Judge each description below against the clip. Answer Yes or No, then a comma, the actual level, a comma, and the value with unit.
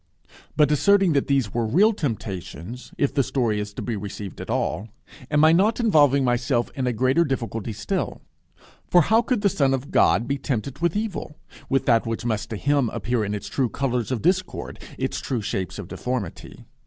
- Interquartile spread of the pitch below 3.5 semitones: No, average, 4.9 semitones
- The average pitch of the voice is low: Yes, low, 130 Hz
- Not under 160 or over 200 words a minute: Yes, average, 195 wpm